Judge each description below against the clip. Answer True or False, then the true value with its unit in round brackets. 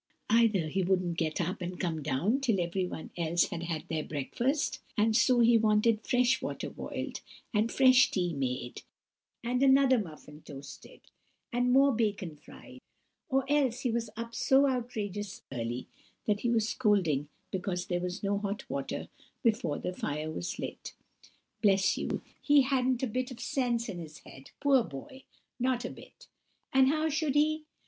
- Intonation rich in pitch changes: True (6.8 semitones)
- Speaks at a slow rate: False (165 wpm)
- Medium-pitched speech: False (215 Hz)